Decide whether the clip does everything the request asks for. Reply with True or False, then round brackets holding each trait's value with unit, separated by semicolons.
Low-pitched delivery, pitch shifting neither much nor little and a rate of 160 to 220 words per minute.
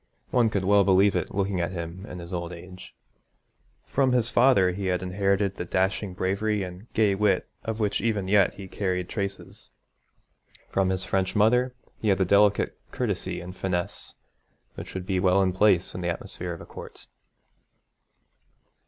False (95 Hz; 2.1 semitones; 170 wpm)